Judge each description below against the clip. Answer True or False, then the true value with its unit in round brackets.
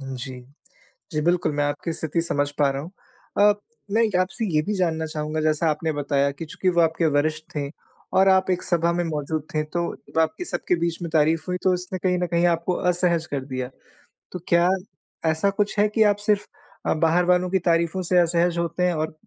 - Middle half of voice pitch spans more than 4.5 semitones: False (2.7 semitones)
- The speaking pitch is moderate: True (170 Hz)